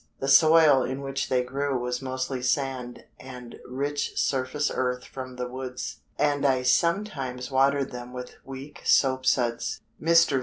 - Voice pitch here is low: Yes, low, 130 Hz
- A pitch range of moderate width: No, narrow, 1.9 semitones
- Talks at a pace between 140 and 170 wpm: Yes, average, 150 wpm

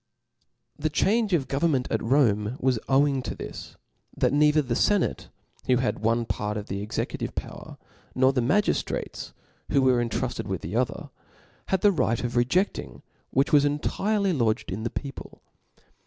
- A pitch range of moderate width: Yes, average, 4.3 semitones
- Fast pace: No, average, 160 wpm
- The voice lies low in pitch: Yes, low, 130 Hz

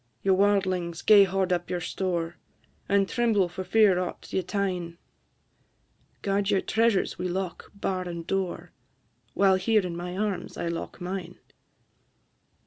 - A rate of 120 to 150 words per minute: Yes, average, 140 wpm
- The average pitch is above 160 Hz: Yes, high, 190 Hz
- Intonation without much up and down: Yes, narrow, 2.0 semitones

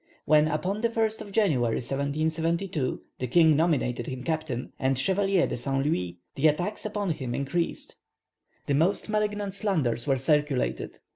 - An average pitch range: No, wide, 6.4 semitones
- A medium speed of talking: Yes, average, 150 wpm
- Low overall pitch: No, medium, 155 Hz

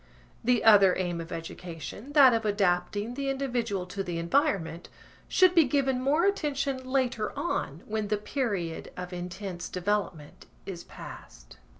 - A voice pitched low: No, high, 210 Hz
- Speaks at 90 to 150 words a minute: Yes, average, 140 wpm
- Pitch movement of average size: No, wide, 6.9 semitones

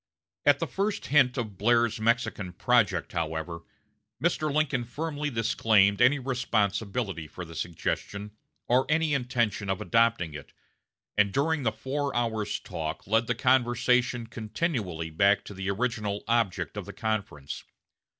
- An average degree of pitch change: Yes, average, 4.3 semitones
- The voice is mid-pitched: No, low, 115 Hz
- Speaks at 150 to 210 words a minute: No, average, 140 wpm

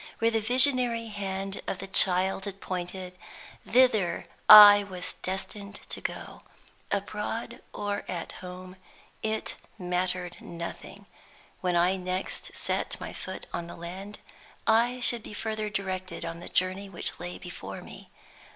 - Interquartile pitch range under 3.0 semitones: Yes, narrow, 2.6 semitones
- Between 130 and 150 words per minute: Yes, average, 140 wpm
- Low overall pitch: No, high, 190 Hz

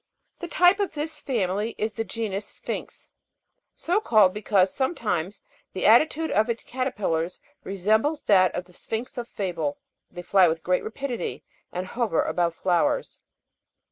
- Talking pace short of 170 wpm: Yes, average, 145 wpm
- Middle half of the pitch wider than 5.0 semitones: Yes, wide, 5.5 semitones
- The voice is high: Yes, high, 210 Hz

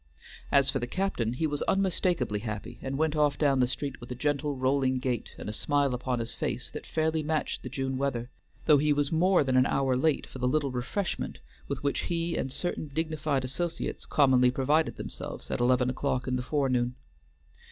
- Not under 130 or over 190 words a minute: No, average, 200 wpm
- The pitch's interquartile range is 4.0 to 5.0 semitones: No, average, 3.3 semitones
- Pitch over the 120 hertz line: Yes, low, 135 Hz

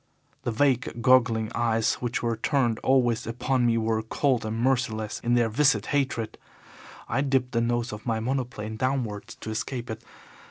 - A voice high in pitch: No, low, 120 Hz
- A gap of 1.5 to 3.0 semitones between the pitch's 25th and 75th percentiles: Yes, narrow, 2.4 semitones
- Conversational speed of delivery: Yes, average, 165 wpm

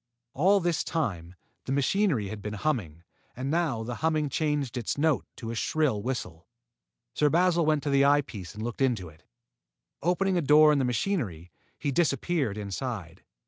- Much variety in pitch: Yes, wide, 6.6 semitones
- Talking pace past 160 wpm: Yes, average, 175 wpm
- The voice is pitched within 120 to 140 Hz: Yes, low, 135 Hz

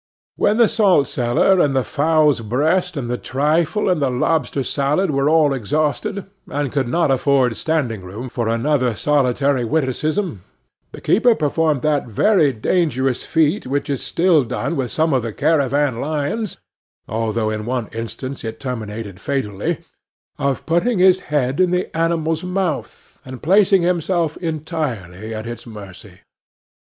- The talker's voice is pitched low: No, medium, 145 Hz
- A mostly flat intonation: No, average, 5.0 semitones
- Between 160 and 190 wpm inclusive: No, average, 150 wpm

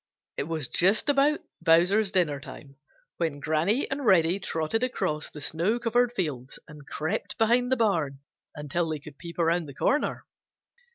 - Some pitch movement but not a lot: No, wide, 6.6 semitones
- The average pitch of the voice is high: No, medium, 170 Hz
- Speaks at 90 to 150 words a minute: No, average, 160 wpm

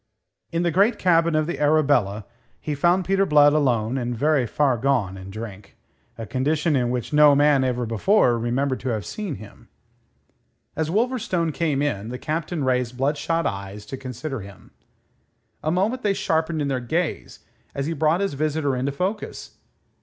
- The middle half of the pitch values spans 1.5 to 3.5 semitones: No, average, 5.0 semitones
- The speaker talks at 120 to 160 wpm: No, average, 170 wpm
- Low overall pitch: No, medium, 145 Hz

